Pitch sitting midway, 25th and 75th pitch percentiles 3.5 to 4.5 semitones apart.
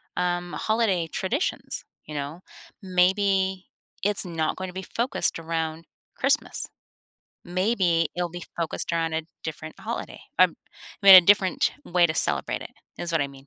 No: medium, 175 Hz; average, 2.7 semitones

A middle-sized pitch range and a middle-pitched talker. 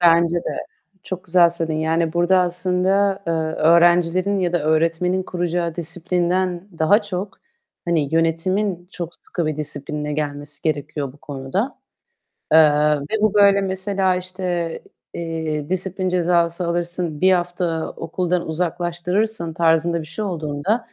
No: narrow, 2.2 semitones; medium, 175 Hz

